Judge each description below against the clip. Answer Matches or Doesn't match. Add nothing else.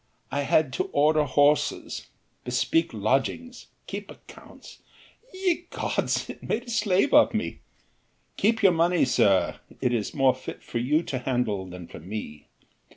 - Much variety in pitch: Matches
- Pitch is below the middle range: Doesn't match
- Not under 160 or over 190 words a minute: Doesn't match